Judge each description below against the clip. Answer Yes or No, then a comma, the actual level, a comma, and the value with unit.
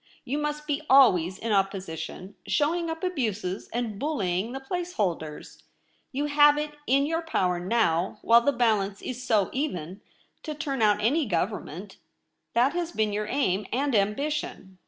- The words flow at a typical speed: Yes, average, 155 wpm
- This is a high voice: Yes, high, 235 Hz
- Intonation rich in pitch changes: Yes, wide, 7.1 semitones